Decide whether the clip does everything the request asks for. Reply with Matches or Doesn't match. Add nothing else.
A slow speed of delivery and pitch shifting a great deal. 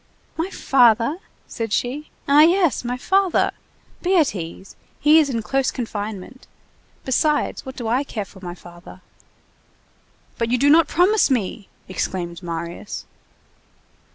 Matches